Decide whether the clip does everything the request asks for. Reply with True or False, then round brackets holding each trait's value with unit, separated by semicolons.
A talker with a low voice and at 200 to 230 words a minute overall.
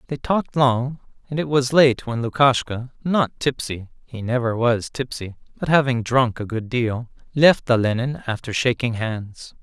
False (125 Hz; 160 wpm)